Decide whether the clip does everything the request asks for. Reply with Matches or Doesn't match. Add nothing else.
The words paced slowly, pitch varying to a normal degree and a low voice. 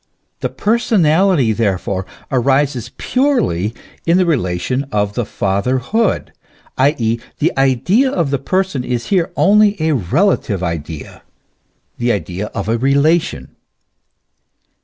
Doesn't match